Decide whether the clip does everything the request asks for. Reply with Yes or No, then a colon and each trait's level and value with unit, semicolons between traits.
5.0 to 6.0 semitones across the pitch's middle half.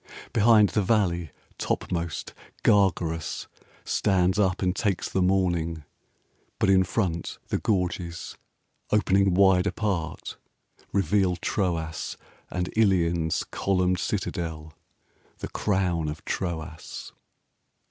No: narrow, 2.6 semitones